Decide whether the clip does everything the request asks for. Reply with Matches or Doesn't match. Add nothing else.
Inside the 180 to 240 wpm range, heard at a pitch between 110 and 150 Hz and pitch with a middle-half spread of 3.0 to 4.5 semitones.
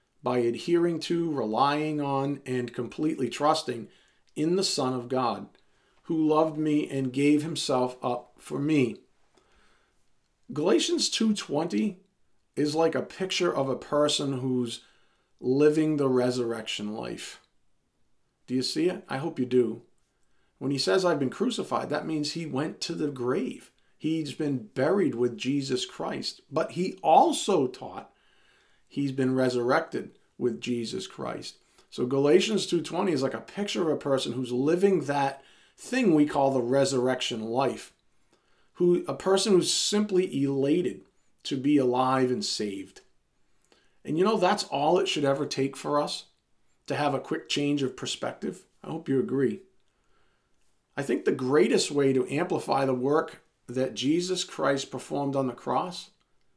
Doesn't match